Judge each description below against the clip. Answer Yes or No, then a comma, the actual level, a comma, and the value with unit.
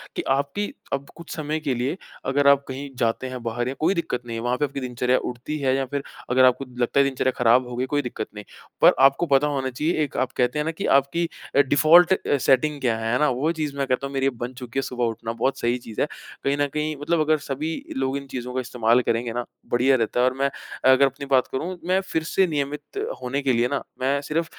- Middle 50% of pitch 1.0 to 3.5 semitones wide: Yes, average, 2.8 semitones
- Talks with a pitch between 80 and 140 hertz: Yes, low, 135 Hz